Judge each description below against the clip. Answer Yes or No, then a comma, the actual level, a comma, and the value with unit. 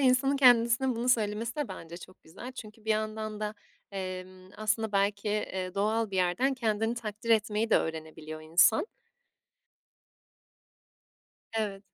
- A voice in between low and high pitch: No, high, 215 Hz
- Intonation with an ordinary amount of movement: Yes, average, 3.5 semitones